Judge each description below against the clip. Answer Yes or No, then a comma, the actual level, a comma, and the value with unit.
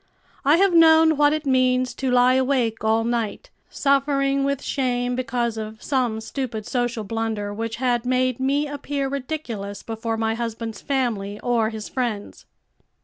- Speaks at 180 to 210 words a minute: No, average, 150 wpm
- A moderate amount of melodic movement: Yes, average, 3.5 semitones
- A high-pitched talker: Yes, very high, 250 Hz